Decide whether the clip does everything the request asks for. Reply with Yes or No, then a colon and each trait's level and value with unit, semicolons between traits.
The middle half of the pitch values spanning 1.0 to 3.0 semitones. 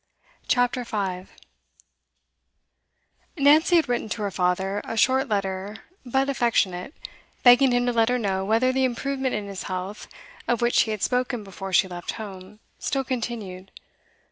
No: average, 4.6 semitones